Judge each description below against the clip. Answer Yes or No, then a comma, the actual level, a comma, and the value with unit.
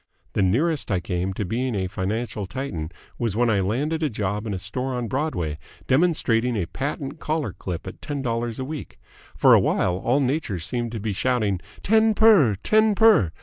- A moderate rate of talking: Yes, average, 190 wpm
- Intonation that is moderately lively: No, wide, 6.8 semitones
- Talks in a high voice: No, low, 120 Hz